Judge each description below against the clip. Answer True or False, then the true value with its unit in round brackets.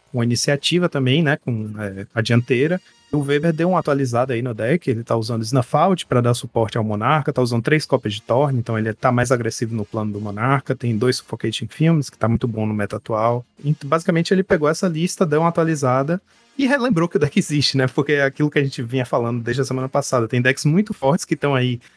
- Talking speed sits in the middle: False (235 wpm)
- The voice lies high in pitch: False (130 Hz)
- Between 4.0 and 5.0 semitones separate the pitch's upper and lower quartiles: True (4.7 semitones)